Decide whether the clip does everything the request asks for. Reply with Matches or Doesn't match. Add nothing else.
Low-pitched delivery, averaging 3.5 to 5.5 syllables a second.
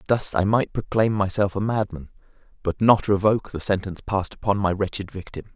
Doesn't match